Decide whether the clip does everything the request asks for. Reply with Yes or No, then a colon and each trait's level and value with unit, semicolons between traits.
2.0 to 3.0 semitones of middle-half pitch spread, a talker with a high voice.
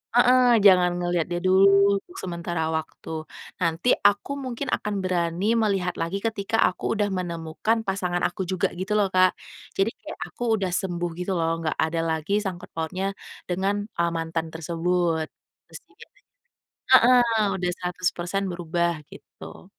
No: average, 2.7 semitones; medium, 180 Hz